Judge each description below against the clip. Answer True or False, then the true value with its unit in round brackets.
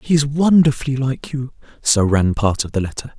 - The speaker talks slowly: False (205 wpm)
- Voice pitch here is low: True (130 Hz)